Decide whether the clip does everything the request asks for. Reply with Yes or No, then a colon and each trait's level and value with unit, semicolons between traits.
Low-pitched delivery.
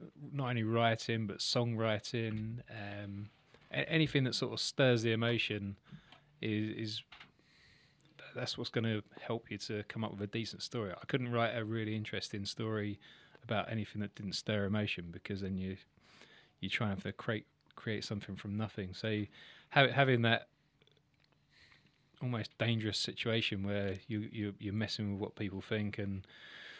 Yes: low, 110 Hz